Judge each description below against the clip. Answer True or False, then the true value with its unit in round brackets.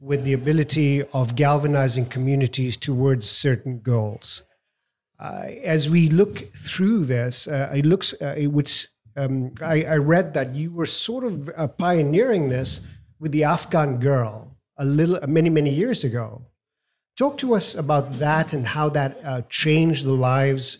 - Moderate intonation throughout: True (3.2 semitones)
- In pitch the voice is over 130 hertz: True (140 Hz)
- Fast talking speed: False (160 wpm)